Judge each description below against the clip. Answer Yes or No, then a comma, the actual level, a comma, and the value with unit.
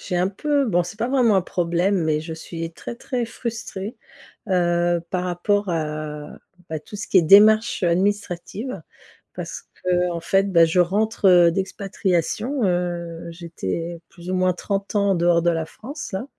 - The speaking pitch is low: No, medium, 180 Hz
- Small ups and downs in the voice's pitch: No, average, 3.2 semitones